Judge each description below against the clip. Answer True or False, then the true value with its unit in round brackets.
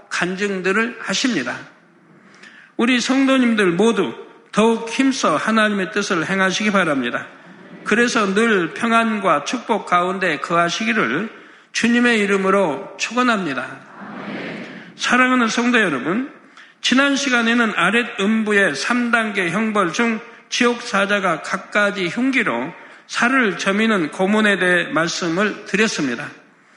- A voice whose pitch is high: True (220 Hz)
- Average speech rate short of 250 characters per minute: False (260 characters per minute)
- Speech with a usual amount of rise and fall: True (3.5 semitones)